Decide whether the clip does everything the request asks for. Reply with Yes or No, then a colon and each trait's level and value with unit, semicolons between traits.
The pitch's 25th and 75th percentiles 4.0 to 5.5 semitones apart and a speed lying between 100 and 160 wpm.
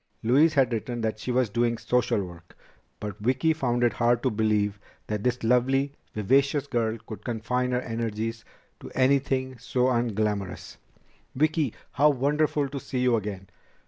No: average, 3.3 semitones; average, 155 wpm